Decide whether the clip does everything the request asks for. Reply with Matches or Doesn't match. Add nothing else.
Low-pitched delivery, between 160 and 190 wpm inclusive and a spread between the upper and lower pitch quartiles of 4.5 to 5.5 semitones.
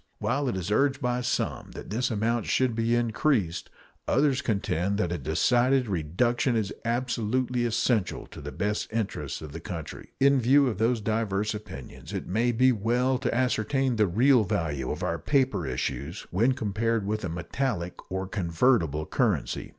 Matches